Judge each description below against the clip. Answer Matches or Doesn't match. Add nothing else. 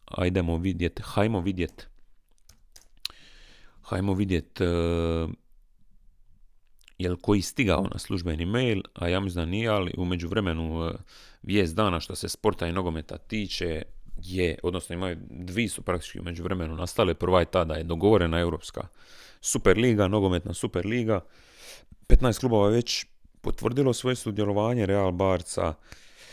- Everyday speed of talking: Matches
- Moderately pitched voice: Doesn't match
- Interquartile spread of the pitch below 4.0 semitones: Matches